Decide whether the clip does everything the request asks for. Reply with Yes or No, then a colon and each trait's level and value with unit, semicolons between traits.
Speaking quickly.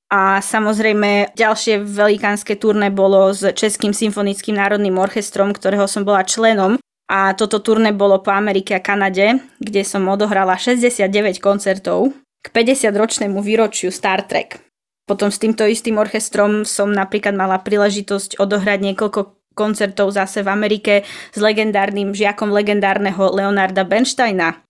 No: average, 130 wpm